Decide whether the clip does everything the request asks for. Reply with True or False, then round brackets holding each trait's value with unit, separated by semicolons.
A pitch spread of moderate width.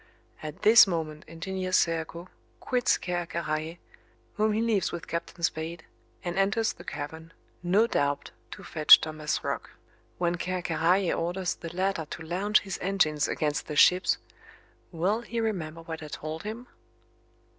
True (3.3 semitones)